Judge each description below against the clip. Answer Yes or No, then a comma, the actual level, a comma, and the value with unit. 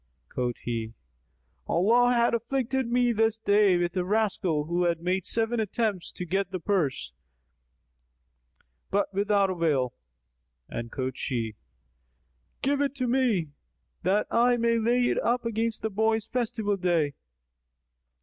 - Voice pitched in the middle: No, high, 205 Hz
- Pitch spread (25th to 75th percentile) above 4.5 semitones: Yes, average, 5.1 semitones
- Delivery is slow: Yes, slow, 130 wpm